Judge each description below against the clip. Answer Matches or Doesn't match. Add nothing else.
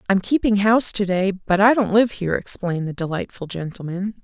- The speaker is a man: Doesn't match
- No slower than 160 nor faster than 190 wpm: Doesn't match